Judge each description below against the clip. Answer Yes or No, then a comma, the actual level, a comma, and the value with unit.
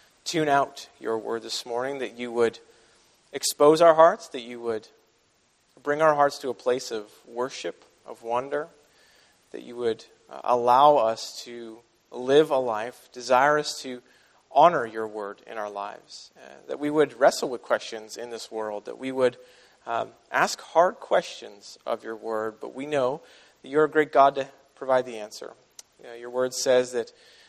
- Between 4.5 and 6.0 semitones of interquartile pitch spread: No, average, 3.9 semitones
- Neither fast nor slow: Yes, average, 175 wpm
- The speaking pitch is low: Yes, low, 125 Hz